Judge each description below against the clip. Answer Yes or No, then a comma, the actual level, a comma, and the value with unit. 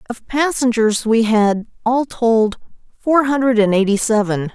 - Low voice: No, high, 230 Hz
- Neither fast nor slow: Yes, average, 145 wpm